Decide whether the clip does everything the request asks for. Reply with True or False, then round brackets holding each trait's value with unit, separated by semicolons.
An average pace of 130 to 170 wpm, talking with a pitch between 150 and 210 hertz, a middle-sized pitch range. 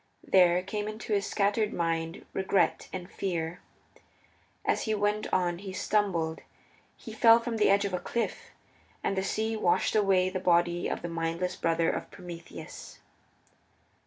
True (155 wpm; 185 Hz; 3.2 semitones)